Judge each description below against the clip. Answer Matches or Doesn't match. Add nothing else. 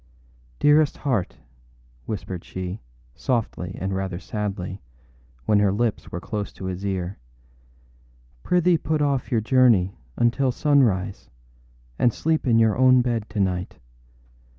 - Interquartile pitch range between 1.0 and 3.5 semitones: Doesn't match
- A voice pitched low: Matches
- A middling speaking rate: Doesn't match